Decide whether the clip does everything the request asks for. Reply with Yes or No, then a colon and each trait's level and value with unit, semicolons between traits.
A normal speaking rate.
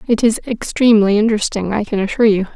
Yes: average, 190 wpm